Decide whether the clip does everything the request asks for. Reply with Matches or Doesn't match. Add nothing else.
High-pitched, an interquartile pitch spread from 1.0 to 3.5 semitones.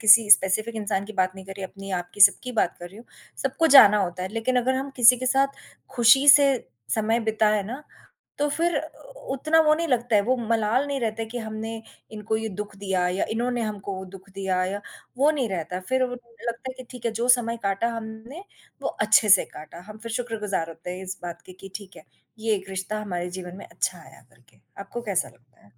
Doesn't match